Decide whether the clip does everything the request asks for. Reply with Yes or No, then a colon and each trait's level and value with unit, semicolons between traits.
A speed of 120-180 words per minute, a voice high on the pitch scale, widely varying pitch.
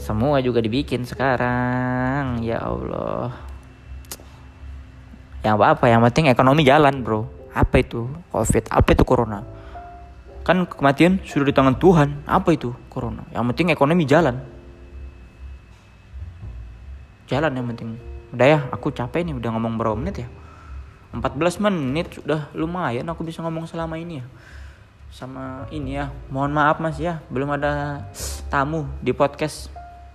No: average, 135 wpm; low, 125 Hz; wide, 6.6 semitones